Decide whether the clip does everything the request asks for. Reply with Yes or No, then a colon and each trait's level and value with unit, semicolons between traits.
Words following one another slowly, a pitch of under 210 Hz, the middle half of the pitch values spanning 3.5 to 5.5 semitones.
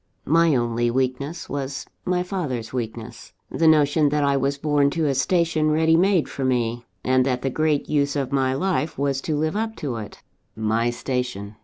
No: average, 185 wpm; medium, 140 Hz; average, 3.8 semitones